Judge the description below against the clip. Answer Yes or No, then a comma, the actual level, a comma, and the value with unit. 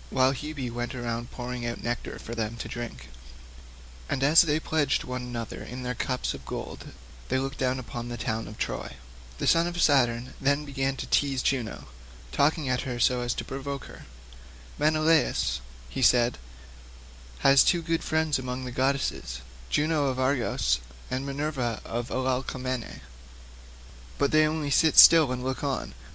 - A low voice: Yes, low, 120 Hz